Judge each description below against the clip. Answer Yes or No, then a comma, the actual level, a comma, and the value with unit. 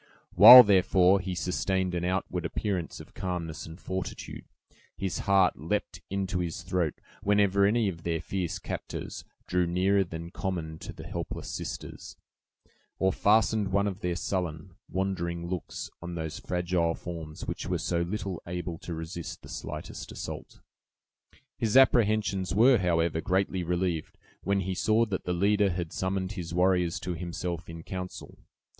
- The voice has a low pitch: Yes, very low, 90 Hz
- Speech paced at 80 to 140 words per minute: No, average, 150 wpm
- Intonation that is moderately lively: No, narrow, 2.2 semitones